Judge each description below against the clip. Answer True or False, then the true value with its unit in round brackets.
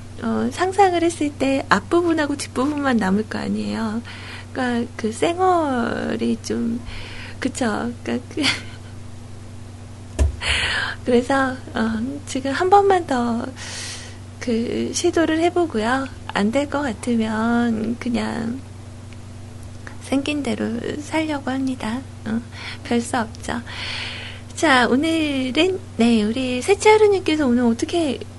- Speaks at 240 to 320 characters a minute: False (210 characters per minute)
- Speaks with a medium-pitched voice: False (230 Hz)